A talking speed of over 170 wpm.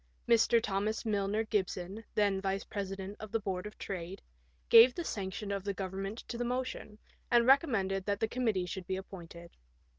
Yes: average, 180 wpm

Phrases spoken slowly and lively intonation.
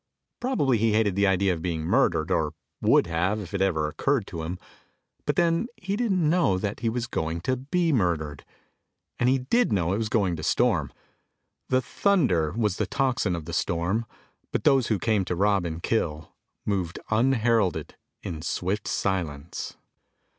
No: average, 175 wpm; wide, 6.7 semitones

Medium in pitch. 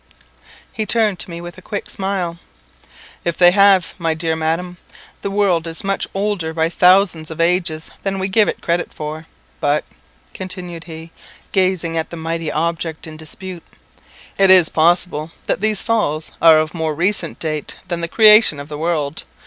Yes: medium, 170 Hz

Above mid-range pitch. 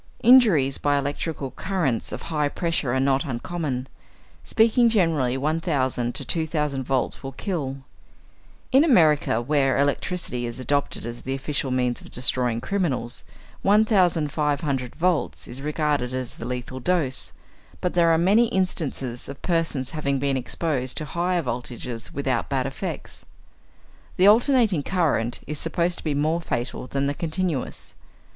No: medium, 145 Hz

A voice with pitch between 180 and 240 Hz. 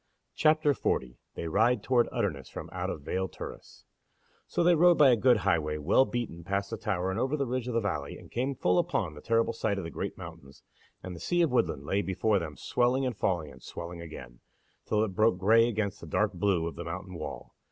No: low, 100 Hz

